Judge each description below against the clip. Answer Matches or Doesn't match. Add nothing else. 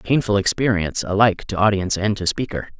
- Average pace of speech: Matches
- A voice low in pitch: Matches